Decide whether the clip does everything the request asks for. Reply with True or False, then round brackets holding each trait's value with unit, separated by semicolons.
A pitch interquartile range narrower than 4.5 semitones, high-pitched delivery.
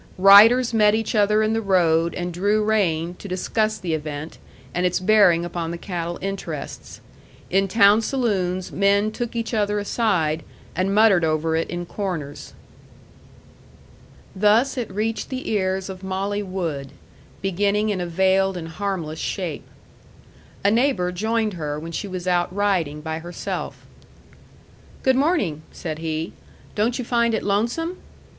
True (3.9 semitones; 195 Hz)